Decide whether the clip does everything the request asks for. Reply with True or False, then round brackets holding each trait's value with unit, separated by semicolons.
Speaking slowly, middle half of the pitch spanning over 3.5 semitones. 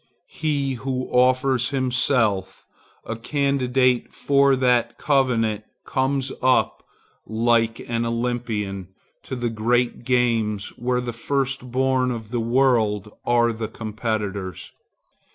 False (110 wpm; 2.4 semitones)